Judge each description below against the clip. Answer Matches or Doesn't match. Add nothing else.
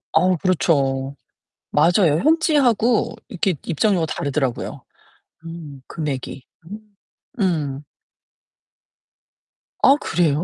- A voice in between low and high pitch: Matches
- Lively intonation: Matches